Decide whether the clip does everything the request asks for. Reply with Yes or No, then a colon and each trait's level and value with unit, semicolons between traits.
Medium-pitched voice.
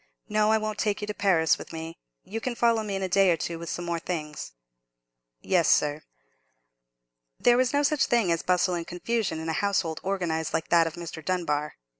Yes: medium, 180 Hz